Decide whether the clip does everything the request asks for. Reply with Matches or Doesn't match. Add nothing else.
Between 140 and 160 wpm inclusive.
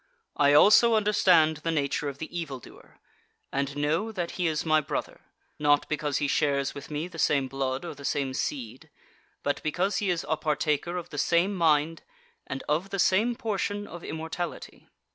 Doesn't match